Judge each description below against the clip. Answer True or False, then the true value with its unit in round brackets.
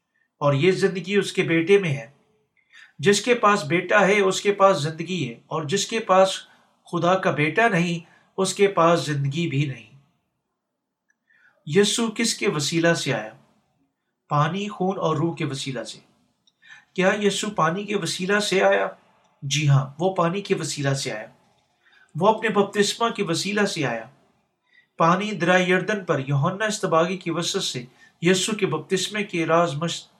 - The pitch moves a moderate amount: True (4.2 semitones)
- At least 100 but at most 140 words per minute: False (160 wpm)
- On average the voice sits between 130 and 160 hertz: False (185 Hz)